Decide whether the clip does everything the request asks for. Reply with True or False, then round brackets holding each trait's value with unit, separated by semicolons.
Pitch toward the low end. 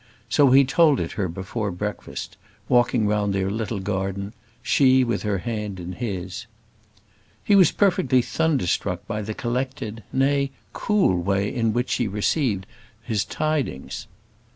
True (110 Hz)